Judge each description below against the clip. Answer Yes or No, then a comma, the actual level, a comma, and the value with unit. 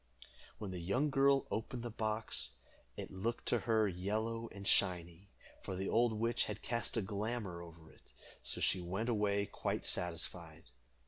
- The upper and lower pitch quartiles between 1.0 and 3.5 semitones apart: No, average, 4.0 semitones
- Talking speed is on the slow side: No, average, 165 wpm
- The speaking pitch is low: Yes, low, 105 Hz